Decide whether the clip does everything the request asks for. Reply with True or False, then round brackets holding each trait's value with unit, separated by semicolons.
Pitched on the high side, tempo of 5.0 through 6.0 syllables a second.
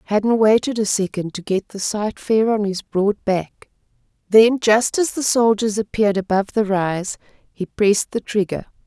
False (210 Hz; 4.7 syllables/s)